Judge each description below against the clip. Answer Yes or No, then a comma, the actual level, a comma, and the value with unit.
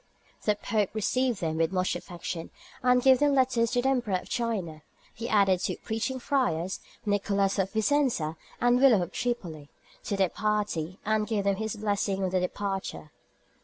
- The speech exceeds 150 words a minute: Yes, average, 170 wpm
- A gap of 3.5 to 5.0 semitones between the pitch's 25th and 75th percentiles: Yes, average, 4.3 semitones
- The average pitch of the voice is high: Yes, high, 205 Hz